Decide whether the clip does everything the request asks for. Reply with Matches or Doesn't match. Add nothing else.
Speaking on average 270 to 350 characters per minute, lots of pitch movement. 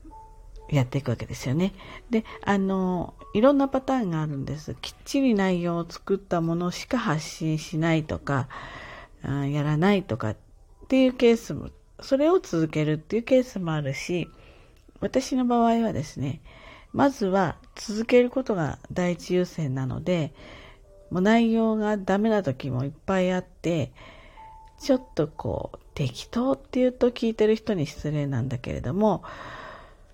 Matches